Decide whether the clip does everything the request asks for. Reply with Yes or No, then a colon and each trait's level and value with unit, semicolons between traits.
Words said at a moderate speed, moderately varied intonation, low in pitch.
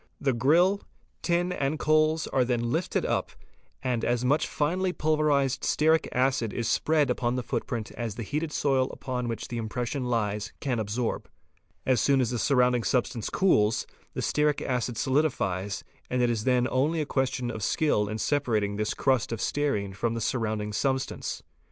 Yes: average, 170 wpm; average, 4.1 semitones; low, 125 Hz